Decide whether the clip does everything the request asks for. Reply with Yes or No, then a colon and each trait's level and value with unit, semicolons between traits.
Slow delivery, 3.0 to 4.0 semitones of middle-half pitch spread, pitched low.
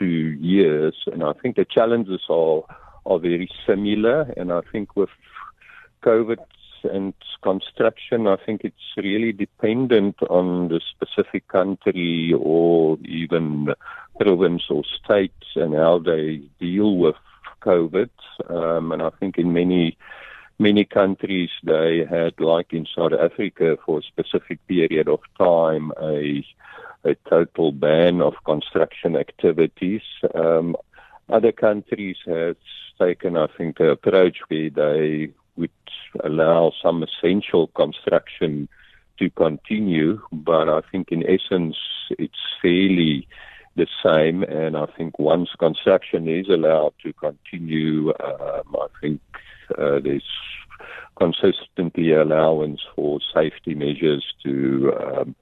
Yes: slow, 120 wpm; average, 3.5 semitones; very low, 85 Hz